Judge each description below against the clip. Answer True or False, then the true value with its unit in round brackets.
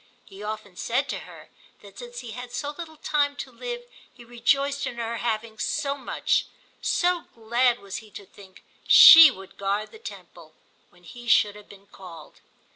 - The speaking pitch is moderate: False (235 Hz)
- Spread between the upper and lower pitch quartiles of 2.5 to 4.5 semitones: False (5.5 semitones)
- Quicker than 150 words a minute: True (180 wpm)